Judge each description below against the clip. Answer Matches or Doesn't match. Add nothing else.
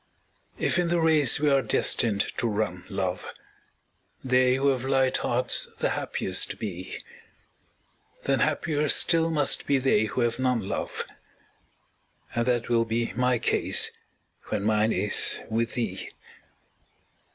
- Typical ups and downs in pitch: Matches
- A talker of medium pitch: Doesn't match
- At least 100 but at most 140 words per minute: Matches